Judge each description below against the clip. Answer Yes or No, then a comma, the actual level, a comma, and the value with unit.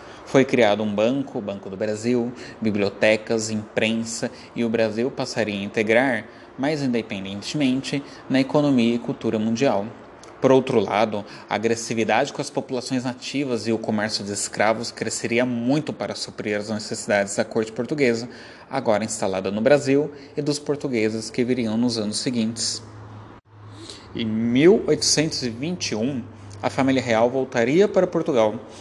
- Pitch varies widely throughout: No, average, 3.4 semitones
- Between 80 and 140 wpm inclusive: Yes, average, 135 wpm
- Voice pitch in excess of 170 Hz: No, low, 115 Hz